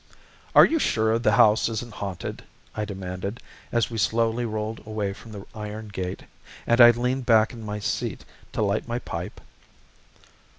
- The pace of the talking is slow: No, average, 165 wpm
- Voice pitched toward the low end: Yes, low, 110 Hz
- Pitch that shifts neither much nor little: No, narrow, 2.2 semitones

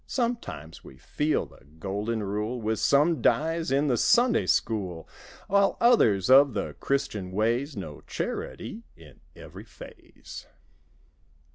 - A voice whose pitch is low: Yes, low, 120 Hz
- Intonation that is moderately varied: No, wide, 7.5 semitones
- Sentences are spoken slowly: Yes, slow, 125 wpm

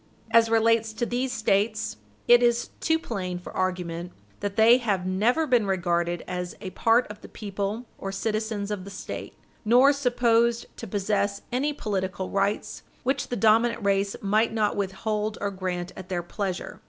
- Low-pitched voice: No, high, 210 Hz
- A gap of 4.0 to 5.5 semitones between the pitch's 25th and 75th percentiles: No, average, 3.3 semitones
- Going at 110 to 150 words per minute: No, average, 165 wpm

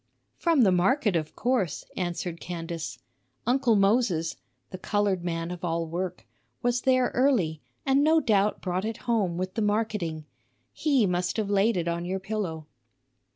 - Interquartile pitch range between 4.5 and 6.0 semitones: Yes, average, 5.1 semitones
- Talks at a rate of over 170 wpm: No, average, 155 wpm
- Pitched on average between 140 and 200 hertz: Yes, high, 190 Hz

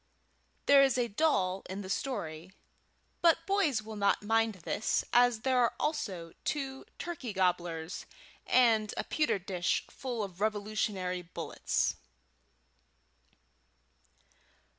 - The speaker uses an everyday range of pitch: No, wide, 5.7 semitones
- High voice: Yes, high, 215 Hz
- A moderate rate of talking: No, slow, 115 wpm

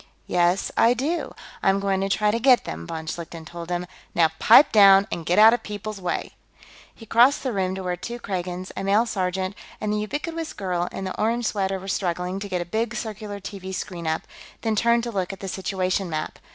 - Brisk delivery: Yes, fast, 220 wpm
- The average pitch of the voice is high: Yes, high, 195 Hz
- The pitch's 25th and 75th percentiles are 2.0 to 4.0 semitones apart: Yes, average, 3.4 semitones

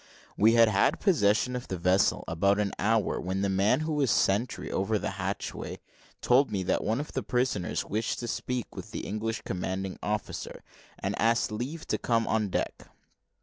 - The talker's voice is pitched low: Yes, low, 110 Hz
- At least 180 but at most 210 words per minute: Yes, average, 185 wpm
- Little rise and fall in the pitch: No, average, 3.8 semitones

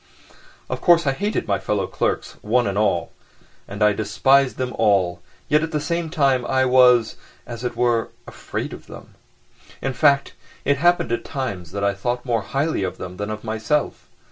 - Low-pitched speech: Yes, low, 120 Hz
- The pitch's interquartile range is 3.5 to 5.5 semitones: Yes, average, 4.9 semitones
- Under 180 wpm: No, average, 185 wpm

